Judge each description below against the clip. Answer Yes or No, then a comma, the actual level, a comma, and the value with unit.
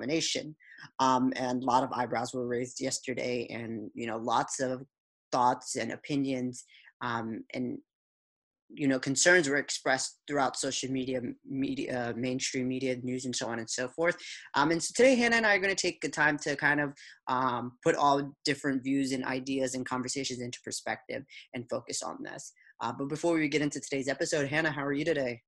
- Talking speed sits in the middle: Yes, average, 190 wpm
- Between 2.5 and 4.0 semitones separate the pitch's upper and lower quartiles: Yes, average, 3.0 semitones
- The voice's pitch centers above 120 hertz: Yes, low, 135 Hz